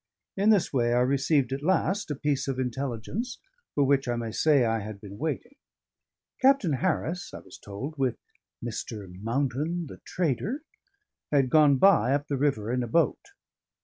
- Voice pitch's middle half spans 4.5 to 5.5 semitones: Yes, average, 4.9 semitones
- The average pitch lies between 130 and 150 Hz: Yes, medium, 140 Hz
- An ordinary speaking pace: Yes, average, 170 wpm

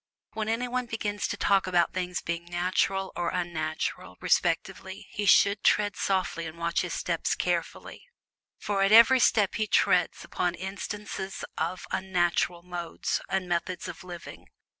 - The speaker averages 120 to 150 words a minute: Yes, average, 145 wpm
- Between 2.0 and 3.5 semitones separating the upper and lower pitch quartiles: Yes, average, 2.8 semitones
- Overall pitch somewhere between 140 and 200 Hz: Yes, medium, 185 Hz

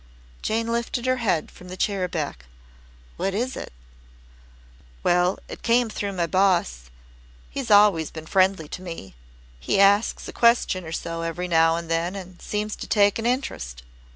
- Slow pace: No, average, 165 wpm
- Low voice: No, medium, 185 Hz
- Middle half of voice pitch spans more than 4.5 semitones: No, average, 4.2 semitones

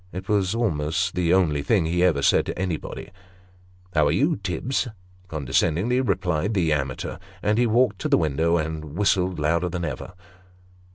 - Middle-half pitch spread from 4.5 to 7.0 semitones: No, average, 3.3 semitones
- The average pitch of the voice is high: No, very low, 90 Hz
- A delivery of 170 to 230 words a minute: Yes, average, 175 wpm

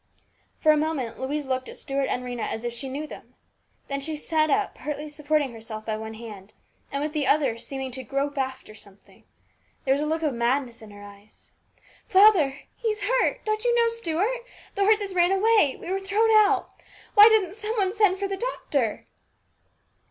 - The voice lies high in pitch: Yes, very high, 300 Hz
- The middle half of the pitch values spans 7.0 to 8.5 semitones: Yes, wide, 7.6 semitones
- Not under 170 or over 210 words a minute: Yes, average, 195 wpm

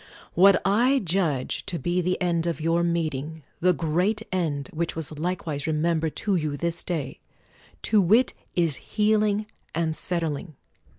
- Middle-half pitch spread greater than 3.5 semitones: No, average, 2.8 semitones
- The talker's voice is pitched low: No, medium, 170 Hz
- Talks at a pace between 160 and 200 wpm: No, average, 145 wpm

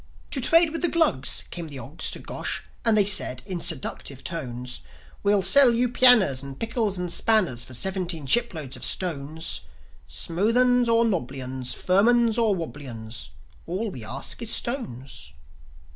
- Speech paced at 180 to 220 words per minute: No, average, 165 wpm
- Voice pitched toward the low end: No, medium, 180 Hz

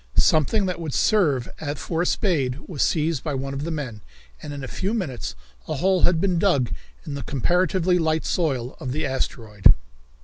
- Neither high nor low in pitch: Yes, medium, 155 Hz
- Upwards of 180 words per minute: Yes, average, 190 wpm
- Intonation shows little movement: No, average, 4.9 semitones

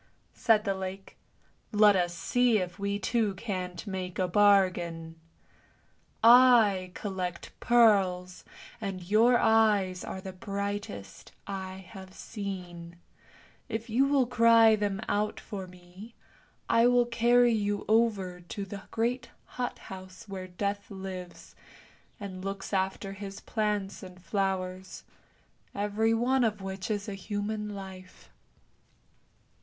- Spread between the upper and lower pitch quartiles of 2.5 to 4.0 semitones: Yes, average, 2.8 semitones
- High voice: Yes, high, 200 Hz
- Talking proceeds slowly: Yes, slow, 130 wpm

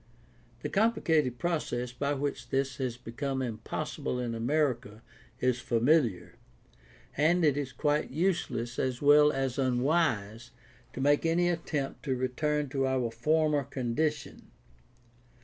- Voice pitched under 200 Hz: Yes, low, 135 Hz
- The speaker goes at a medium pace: No, slow, 125 wpm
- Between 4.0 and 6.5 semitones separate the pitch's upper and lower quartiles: No, average, 3.6 semitones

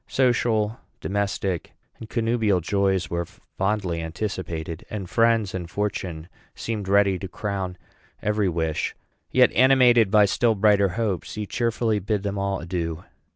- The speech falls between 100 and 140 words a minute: Yes, slow, 135 wpm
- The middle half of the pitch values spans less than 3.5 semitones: Yes, average, 3.1 semitones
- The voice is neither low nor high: No, low, 100 Hz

